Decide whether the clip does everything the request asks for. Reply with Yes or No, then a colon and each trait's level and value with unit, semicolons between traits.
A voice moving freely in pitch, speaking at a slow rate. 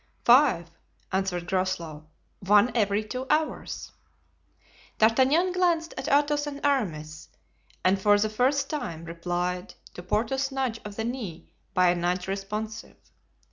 Yes: wide, 6.8 semitones; slow, 130 wpm